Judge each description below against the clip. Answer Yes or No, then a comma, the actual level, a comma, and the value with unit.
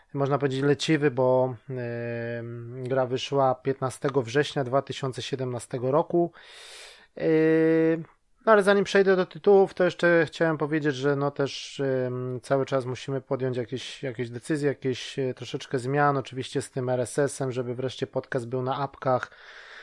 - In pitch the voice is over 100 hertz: Yes, low, 135 Hz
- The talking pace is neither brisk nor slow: Yes, average, 140 wpm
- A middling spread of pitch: Yes, average, 3.0 semitones